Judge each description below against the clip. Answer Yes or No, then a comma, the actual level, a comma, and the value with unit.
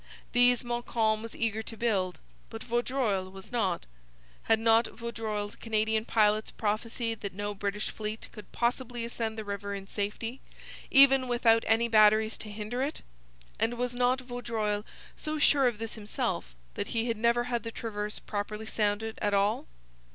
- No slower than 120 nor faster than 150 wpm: No, average, 160 wpm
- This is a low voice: No, high, 225 Hz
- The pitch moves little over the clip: Yes, narrow, 2.3 semitones